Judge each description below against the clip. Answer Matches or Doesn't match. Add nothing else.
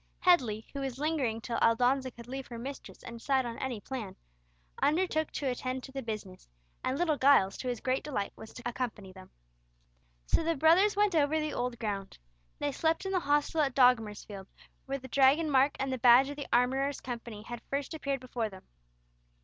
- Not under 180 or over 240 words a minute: Matches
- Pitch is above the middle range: Matches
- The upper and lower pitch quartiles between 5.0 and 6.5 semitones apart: Doesn't match